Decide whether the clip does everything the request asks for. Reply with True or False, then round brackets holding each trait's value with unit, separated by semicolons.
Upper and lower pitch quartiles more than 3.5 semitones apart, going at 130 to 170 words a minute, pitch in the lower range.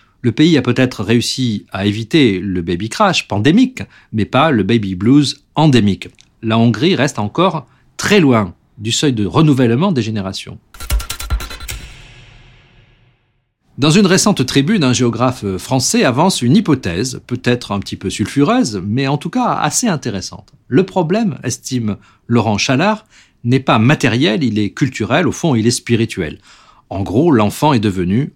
True (4.6 semitones; 150 wpm; 120 Hz)